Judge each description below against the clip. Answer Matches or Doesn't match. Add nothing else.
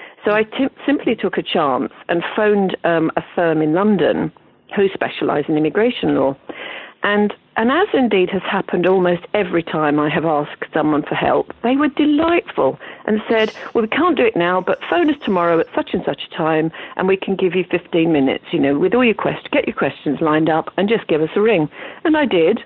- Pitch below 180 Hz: Doesn't match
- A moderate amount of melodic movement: Doesn't match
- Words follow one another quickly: Matches